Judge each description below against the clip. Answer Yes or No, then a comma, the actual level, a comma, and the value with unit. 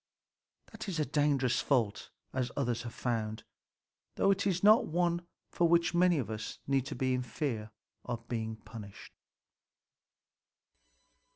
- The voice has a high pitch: No, low, 135 Hz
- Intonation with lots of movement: Yes, wide, 7.2 semitones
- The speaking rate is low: Yes, slow, 120 wpm